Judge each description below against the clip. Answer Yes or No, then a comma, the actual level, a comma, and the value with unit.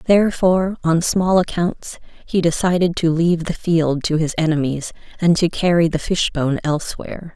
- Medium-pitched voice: Yes, medium, 170 Hz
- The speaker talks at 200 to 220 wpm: No, average, 155 wpm